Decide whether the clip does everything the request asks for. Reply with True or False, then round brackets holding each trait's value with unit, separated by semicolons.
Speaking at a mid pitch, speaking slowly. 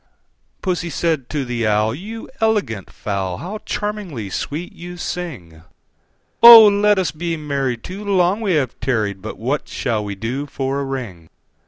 False (145 Hz; 165 wpm)